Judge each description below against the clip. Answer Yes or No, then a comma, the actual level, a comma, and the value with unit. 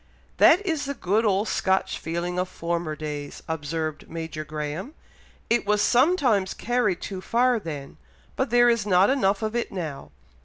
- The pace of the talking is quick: No, average, 160 wpm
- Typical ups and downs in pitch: No, wide, 6.6 semitones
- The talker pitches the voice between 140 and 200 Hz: Yes, high, 190 Hz